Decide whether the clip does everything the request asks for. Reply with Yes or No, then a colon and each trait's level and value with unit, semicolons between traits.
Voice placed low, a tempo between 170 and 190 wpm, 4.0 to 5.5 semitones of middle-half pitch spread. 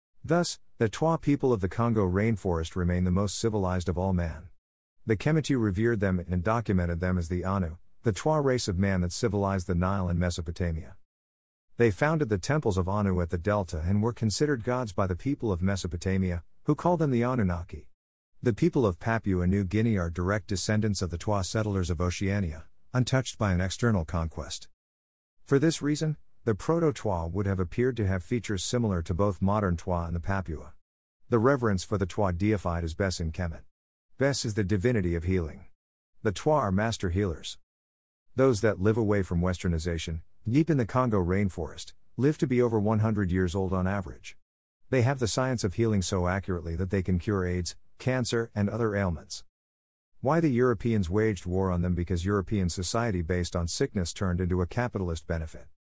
Yes: very low, 95 Hz; average, 185 wpm; average, 4.3 semitones